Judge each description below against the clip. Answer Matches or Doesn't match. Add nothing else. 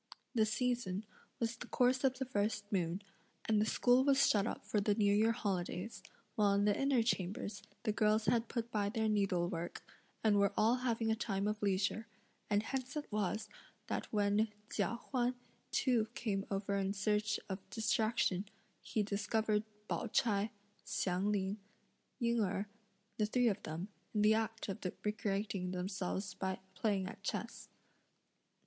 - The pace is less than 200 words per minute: Matches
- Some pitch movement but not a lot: Doesn't match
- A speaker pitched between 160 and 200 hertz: Doesn't match